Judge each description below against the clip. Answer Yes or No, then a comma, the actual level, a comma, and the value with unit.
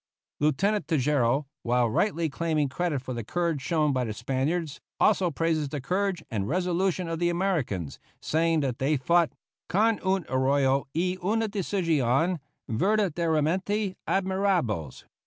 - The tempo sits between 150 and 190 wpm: No, slow, 135 wpm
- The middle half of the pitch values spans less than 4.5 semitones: No, wide, 5.5 semitones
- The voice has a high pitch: No, medium, 165 Hz